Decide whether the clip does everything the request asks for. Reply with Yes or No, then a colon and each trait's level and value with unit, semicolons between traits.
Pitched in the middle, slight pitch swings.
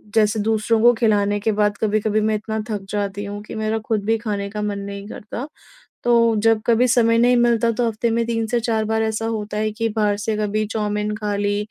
No: high, 215 Hz; narrow, 1.5 semitones